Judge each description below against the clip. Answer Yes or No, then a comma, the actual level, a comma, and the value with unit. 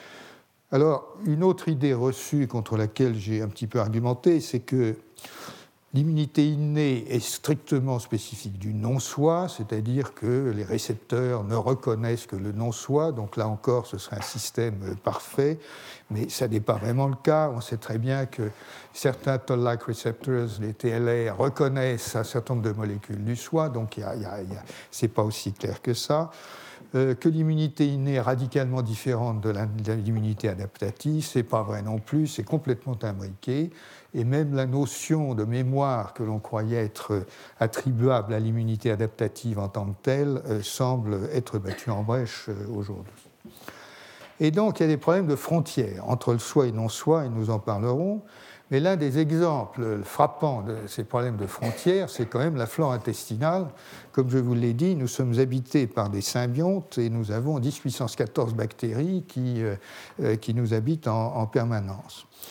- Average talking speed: Yes, average, 170 wpm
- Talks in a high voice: No, low, 120 Hz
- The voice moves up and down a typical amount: Yes, average, 4.0 semitones